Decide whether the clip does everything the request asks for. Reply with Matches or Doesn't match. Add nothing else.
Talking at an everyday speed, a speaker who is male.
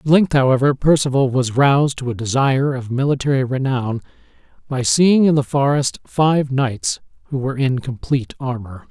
Matches